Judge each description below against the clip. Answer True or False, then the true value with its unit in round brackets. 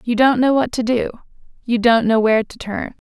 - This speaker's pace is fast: True (215 wpm)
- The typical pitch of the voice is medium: False (235 Hz)